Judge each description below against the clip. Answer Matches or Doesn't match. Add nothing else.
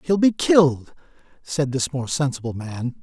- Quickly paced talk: Doesn't match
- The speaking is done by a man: Matches